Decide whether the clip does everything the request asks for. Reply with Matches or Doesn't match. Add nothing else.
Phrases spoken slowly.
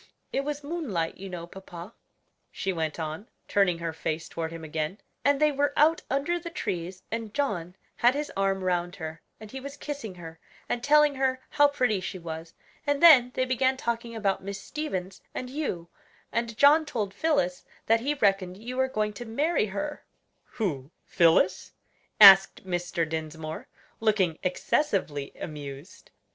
Doesn't match